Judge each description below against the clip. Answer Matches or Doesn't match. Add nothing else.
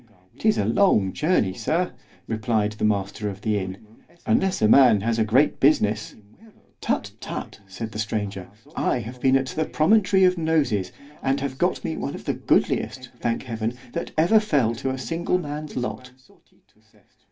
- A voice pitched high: Doesn't match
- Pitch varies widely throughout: Matches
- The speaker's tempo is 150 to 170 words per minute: Matches